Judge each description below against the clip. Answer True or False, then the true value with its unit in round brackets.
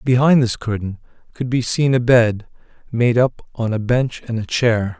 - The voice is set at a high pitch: False (120 Hz)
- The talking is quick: False (190 wpm)